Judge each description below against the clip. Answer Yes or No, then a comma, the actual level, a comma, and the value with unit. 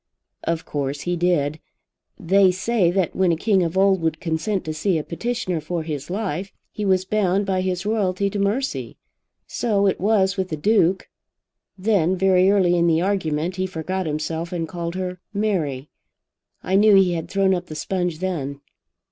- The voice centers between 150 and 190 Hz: Yes, medium, 185 Hz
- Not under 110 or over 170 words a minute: No, average, 180 wpm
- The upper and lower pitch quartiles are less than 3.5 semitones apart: Yes, average, 2.9 semitones